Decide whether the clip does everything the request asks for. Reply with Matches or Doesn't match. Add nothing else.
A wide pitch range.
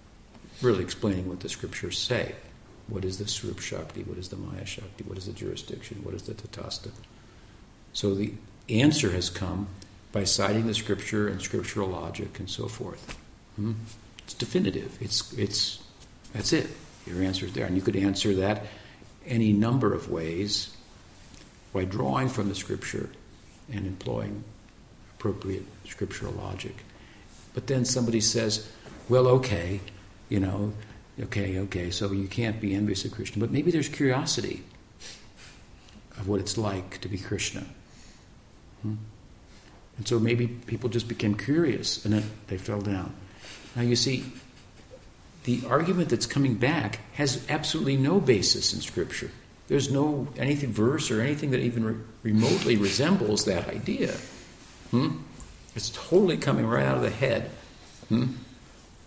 Doesn't match